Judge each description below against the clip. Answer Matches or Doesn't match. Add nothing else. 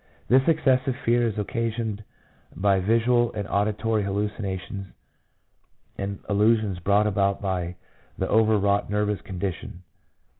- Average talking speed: Doesn't match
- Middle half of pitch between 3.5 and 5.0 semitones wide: Doesn't match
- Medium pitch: Doesn't match